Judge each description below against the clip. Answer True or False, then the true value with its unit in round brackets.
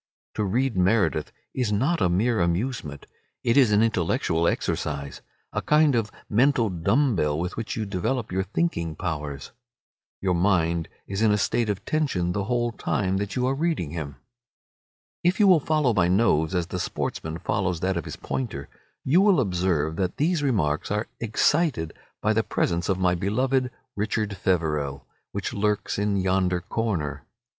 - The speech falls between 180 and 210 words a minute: False (165 wpm)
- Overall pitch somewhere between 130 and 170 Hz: False (100 Hz)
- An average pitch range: False (5.7 semitones)